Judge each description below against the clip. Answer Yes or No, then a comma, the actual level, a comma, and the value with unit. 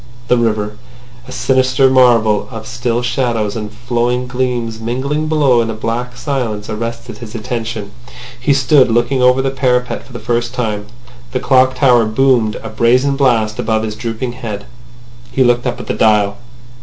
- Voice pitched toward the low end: Yes, low, 120 Hz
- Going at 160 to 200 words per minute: Yes, average, 170 wpm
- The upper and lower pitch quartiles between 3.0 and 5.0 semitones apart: No, narrow, 2.5 semitones